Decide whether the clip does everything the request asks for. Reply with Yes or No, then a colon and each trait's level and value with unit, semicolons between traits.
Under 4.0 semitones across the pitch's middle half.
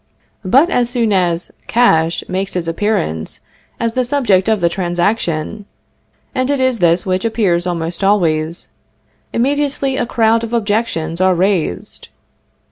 No: average, 5.3 semitones